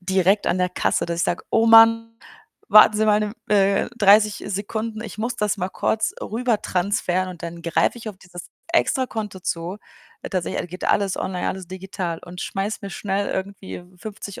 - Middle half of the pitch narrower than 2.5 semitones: No, average, 2.9 semitones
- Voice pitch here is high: Yes, high, 200 Hz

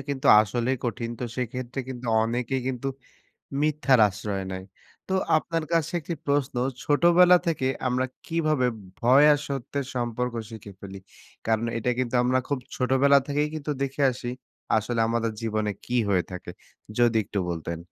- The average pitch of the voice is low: Yes, low, 125 Hz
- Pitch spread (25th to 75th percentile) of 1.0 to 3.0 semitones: No, average, 3.6 semitones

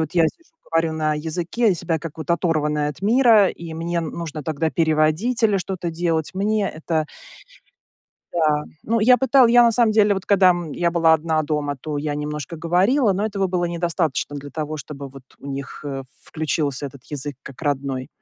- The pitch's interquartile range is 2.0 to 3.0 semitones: No, average, 4.1 semitones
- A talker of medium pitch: Yes, medium, 165 Hz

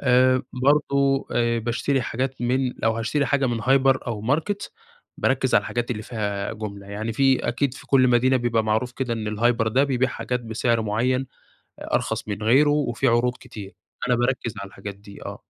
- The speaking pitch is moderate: No, low, 120 Hz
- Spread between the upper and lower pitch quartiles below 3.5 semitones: Yes, average, 2.9 semitones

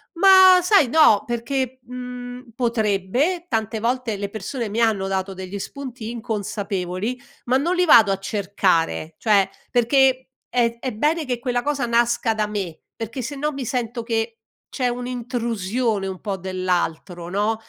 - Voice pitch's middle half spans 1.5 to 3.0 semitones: No, average, 3.9 semitones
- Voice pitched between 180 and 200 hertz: No, high, 230 Hz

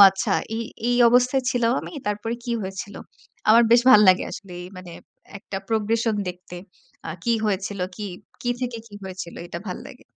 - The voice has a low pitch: No, high, 210 Hz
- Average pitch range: Yes, average, 3.6 semitones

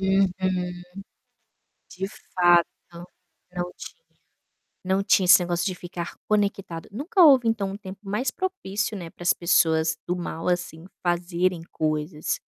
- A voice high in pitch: No, medium, 180 Hz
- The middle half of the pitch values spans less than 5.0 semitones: Yes, narrow, 2.6 semitones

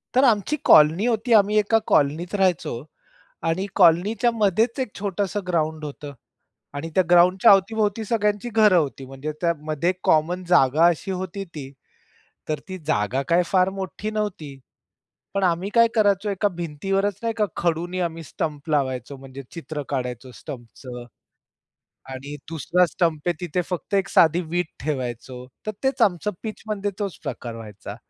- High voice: No, medium, 175 Hz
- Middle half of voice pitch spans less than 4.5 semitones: No, wide, 5.5 semitones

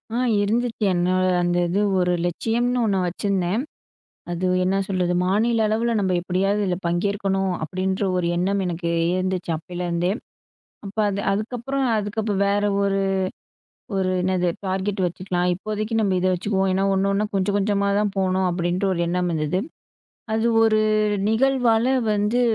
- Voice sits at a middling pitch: No, high, 195 Hz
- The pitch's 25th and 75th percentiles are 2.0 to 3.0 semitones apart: Yes, average, 2.7 semitones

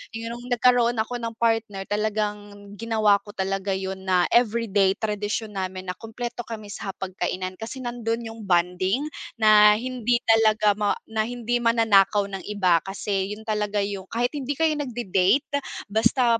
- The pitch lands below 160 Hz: No, high, 215 Hz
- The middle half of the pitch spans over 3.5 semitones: No, average, 3.0 semitones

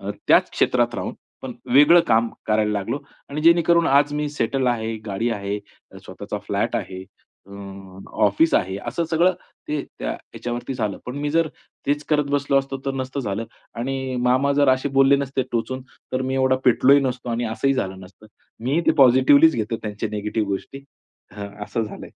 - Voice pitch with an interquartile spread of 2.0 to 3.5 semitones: No, average, 4.1 semitones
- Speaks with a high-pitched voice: No, low, 130 Hz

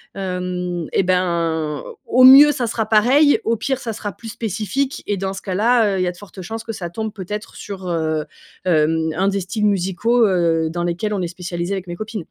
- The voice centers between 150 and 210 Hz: Yes, high, 190 Hz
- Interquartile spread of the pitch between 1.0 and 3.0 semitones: No, average, 4.1 semitones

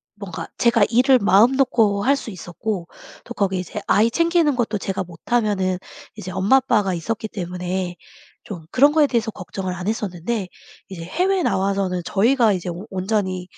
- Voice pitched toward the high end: Yes, high, 205 Hz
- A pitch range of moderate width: Yes, average, 4.2 semitones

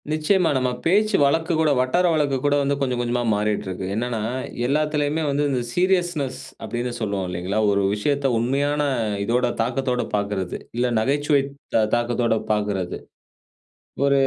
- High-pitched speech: No, low, 130 Hz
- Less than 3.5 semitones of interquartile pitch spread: No, average, 4.8 semitones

